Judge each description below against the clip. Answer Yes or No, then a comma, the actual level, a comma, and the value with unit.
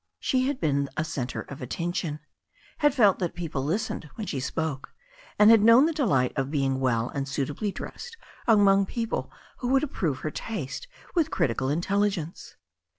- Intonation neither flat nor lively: No, wide, 8.3 semitones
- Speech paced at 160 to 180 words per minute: Yes, average, 165 wpm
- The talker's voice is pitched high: No, medium, 170 Hz